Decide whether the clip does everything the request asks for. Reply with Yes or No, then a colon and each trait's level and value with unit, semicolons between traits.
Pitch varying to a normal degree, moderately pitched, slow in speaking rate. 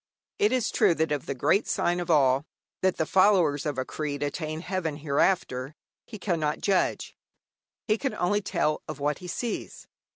No: average, 4.5 semitones; medium, 160 Hz; average, 175 wpm